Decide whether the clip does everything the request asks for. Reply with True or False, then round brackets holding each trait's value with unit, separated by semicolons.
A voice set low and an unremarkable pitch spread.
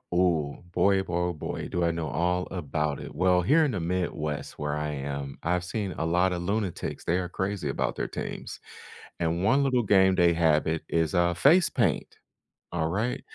True (85 Hz; 3.1 semitones)